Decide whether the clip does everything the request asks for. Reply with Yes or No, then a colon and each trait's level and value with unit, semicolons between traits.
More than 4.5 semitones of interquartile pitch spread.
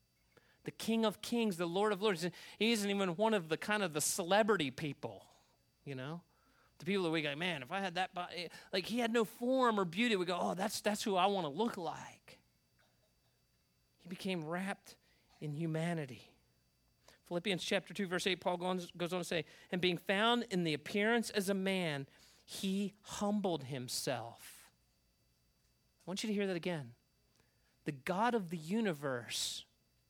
Yes: average, 5.1 semitones